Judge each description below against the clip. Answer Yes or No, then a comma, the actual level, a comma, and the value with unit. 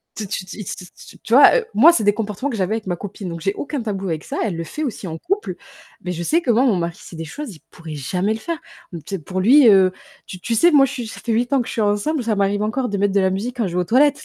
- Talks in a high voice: Yes, high, 210 Hz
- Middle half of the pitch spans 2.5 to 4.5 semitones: No, average, 5.1 semitones